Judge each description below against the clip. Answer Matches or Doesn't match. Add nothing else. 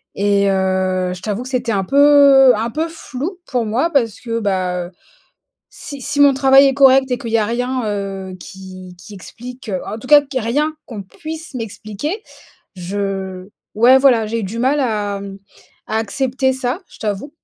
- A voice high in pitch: Matches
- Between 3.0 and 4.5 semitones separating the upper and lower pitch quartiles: Doesn't match